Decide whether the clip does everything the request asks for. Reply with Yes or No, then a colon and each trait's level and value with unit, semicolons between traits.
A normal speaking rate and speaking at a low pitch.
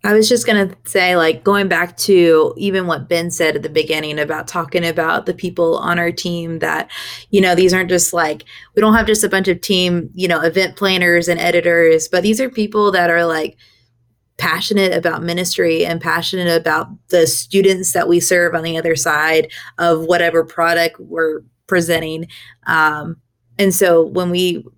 No: average, 190 wpm; medium, 170 Hz